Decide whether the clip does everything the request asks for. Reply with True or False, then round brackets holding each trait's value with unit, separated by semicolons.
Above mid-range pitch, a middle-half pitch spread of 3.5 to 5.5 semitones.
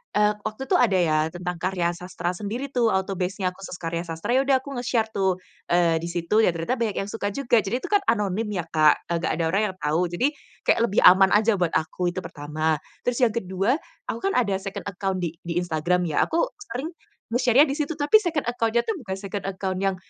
True (195 Hz; 5.1 semitones)